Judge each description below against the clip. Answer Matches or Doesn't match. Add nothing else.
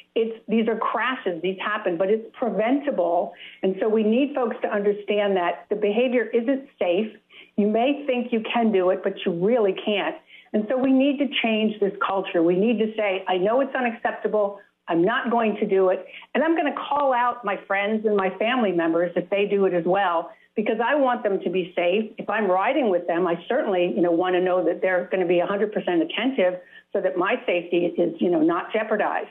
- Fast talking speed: Matches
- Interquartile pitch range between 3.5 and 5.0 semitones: Matches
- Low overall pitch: Doesn't match